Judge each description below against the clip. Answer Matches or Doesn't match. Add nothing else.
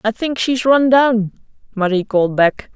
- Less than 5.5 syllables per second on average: Matches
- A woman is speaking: Matches